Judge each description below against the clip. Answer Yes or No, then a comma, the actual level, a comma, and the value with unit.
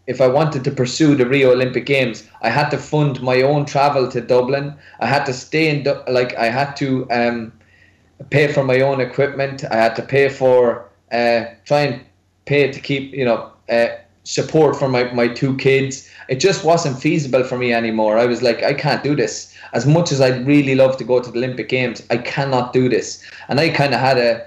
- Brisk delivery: Yes, fast, 220 wpm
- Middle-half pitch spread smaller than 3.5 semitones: Yes, average, 2.8 semitones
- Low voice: Yes, low, 130 Hz